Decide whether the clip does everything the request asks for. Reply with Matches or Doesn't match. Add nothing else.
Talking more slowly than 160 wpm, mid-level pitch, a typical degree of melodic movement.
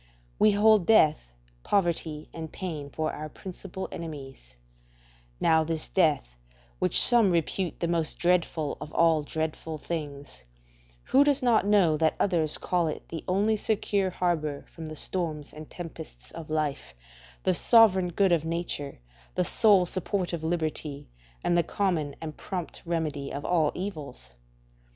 Matches